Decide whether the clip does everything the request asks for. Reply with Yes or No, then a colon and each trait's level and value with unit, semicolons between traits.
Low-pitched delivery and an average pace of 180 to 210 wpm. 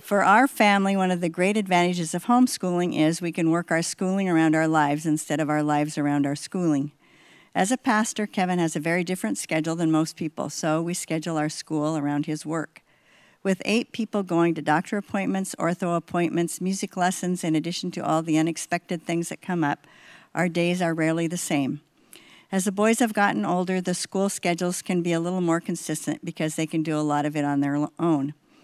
No: medium, 170 Hz; fast, 205 wpm